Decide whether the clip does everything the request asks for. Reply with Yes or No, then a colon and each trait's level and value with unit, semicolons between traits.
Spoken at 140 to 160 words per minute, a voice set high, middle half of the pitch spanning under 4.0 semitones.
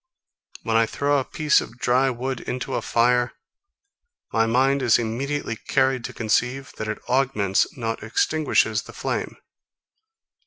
No: average, 145 wpm; low, 125 Hz; average, 2.9 semitones